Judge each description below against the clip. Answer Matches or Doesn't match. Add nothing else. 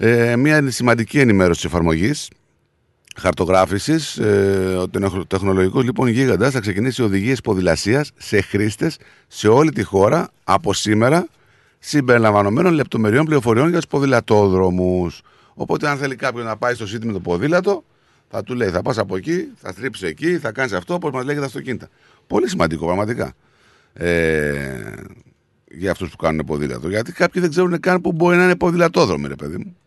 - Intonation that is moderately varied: Doesn't match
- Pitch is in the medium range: Doesn't match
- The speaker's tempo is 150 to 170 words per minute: Matches